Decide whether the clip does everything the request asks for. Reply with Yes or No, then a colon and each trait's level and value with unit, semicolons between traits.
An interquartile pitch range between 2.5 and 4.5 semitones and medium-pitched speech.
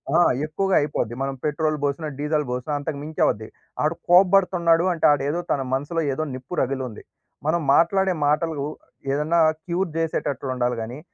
Yes: average, 3.6 semitones; medium, 150 Hz